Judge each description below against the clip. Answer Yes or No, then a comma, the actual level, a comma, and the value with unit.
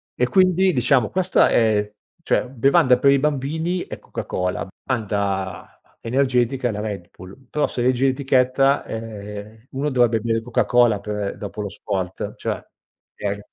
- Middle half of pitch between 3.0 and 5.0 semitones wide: Yes, average, 4.5 semitones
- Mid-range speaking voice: No, low, 120 Hz